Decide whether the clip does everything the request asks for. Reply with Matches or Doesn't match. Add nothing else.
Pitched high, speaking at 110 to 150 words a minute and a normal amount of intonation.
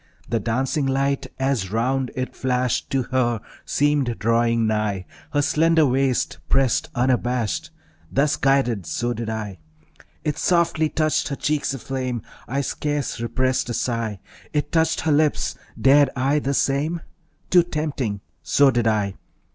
Doesn't match